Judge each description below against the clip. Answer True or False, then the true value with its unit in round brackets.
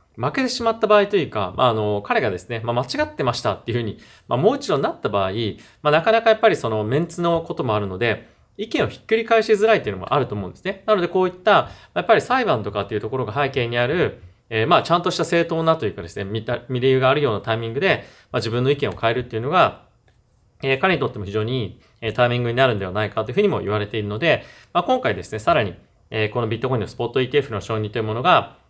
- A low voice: True (125 Hz)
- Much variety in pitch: True (7.7 semitones)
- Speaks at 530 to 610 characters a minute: True (540 characters per minute)